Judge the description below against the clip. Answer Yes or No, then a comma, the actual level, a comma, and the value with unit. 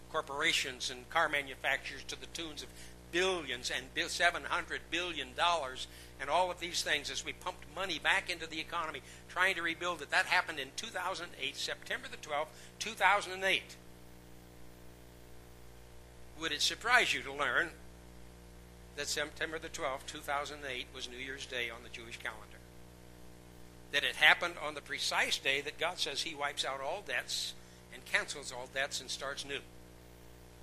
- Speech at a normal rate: Yes, average, 155 wpm